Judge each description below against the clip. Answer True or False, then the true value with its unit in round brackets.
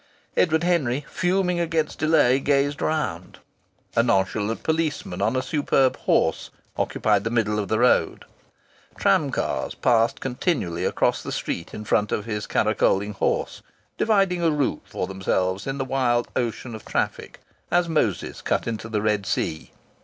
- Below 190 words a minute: True (155 wpm)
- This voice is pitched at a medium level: False (120 Hz)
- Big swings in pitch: True (6.7 semitones)